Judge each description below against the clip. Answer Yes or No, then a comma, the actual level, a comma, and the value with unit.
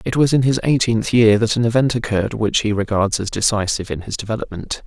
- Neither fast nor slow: No, fast, 220 wpm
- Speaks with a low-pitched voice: Yes, low, 110 Hz